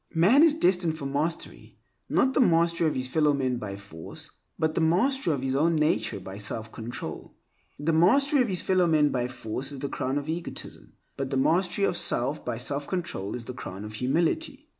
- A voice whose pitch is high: No, medium, 150 Hz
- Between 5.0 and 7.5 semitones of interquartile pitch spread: Yes, wide, 5.5 semitones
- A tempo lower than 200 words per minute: No, fast, 205 wpm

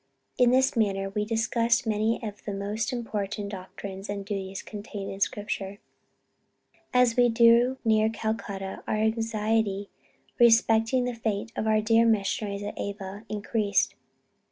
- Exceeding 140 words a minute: No, slow, 135 wpm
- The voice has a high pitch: Yes, high, 215 Hz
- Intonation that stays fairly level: Yes, narrow, 2.2 semitones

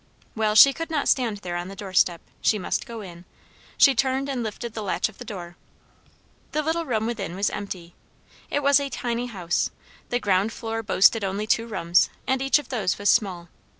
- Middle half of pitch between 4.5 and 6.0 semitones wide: Yes, average, 4.9 semitones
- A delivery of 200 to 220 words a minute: Yes, fast, 205 wpm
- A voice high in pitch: Yes, high, 220 Hz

